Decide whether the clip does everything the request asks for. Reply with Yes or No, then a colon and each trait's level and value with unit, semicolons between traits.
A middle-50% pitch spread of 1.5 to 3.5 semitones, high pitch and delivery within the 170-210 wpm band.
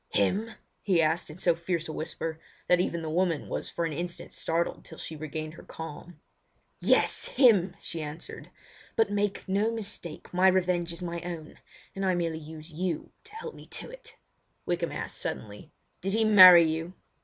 No: average, 2.8 semitones; medium, 175 Hz; average, 180 wpm